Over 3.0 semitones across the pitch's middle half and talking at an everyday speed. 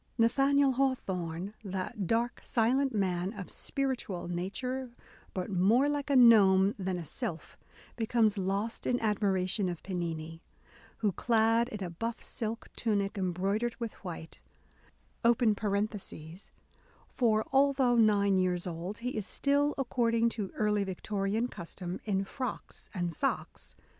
No: average, 4.3 semitones; slow, 125 wpm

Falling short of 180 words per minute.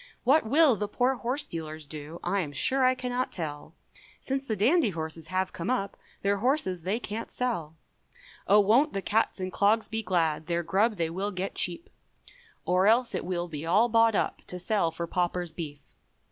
No: average, 190 wpm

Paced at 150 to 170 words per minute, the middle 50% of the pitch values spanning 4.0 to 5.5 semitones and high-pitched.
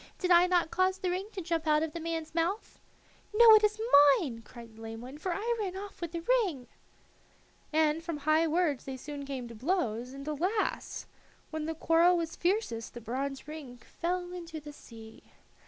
No: average, 195 wpm; average, 4.7 semitones; very high, 320 Hz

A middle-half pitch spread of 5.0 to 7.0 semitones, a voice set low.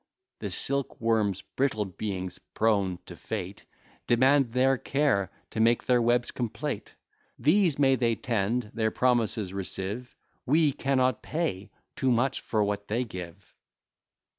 No: average, 4.2 semitones; low, 115 Hz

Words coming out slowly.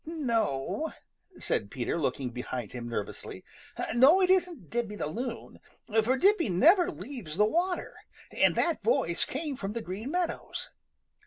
No: average, 145 wpm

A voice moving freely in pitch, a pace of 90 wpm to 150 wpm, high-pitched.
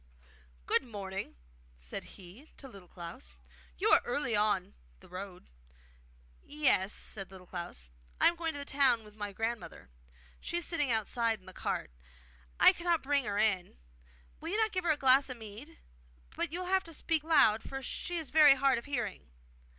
No: wide, 7.3 semitones; average, 185 wpm; high, 240 Hz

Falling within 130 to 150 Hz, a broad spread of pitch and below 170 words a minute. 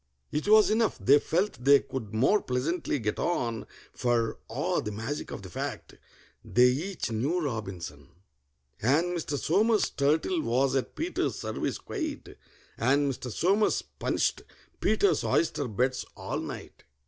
Yes: medium, 140 Hz; wide, 6.9 semitones; average, 140 wpm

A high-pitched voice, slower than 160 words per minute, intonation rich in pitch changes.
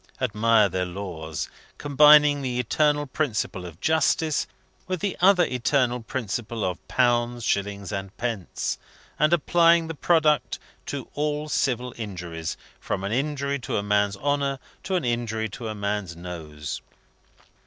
No: low, 120 Hz; average, 140 wpm; wide, 6.5 semitones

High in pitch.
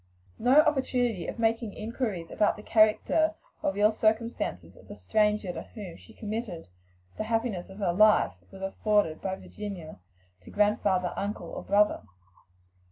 Yes: high, 210 Hz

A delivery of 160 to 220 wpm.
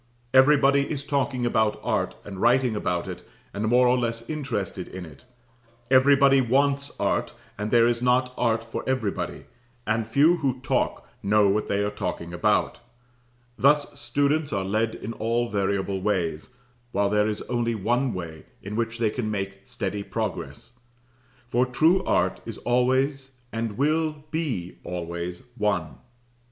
No: average, 150 wpm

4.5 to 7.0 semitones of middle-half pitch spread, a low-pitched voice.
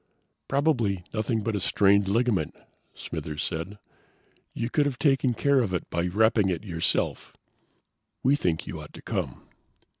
Yes: wide, 5.6 semitones; low, 105 Hz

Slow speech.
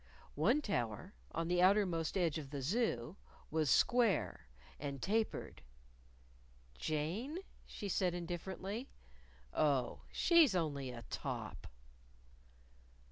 Yes: slow, 105 wpm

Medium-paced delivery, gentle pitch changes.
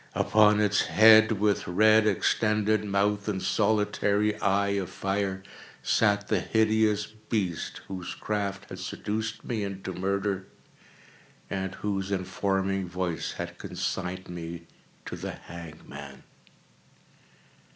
No: slow, 110 wpm; narrow, 2.0 semitones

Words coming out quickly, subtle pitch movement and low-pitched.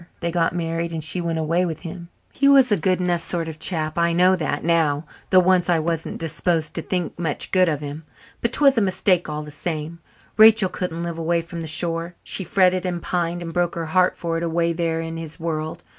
No: fast, 230 wpm; narrow, 1.8 semitones; medium, 170 Hz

